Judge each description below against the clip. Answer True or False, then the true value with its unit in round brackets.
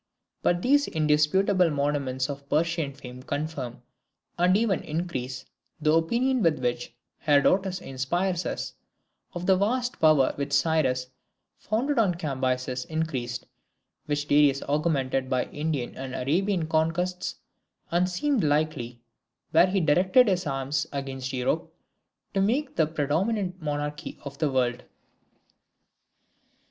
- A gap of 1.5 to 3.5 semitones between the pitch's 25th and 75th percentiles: False (5.0 semitones)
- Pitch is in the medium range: True (155 Hz)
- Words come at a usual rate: False (120 wpm)